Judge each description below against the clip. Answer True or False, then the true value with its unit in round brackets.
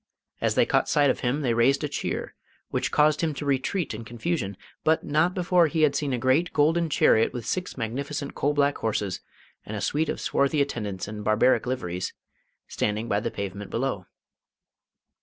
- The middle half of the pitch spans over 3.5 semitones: True (5.5 semitones)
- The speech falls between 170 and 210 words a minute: True (185 wpm)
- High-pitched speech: False (135 Hz)